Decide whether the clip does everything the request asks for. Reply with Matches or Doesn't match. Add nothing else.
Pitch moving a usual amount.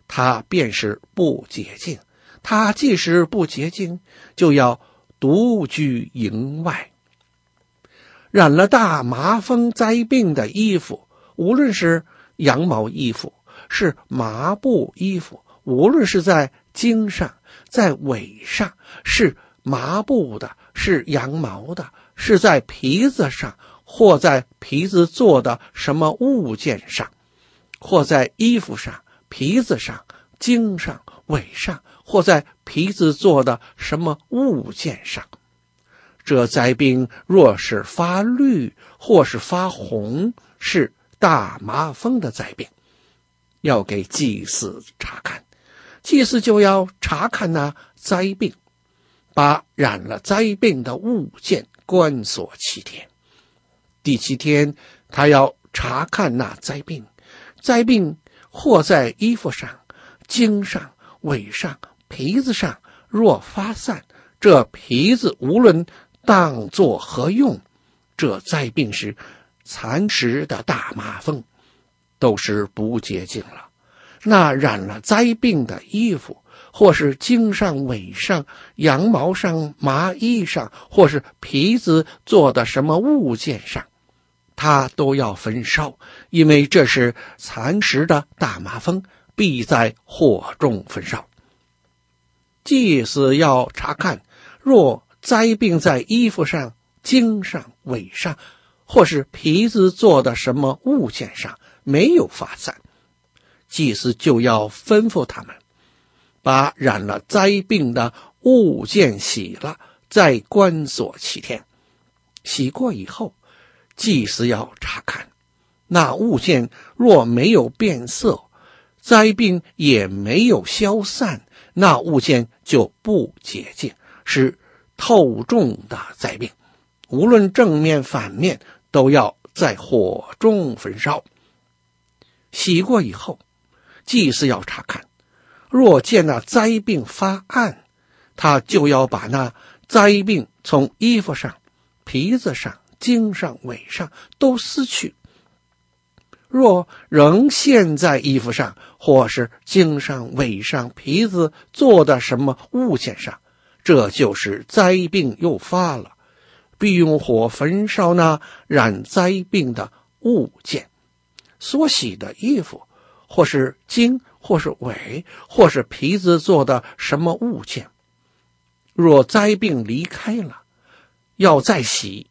Doesn't match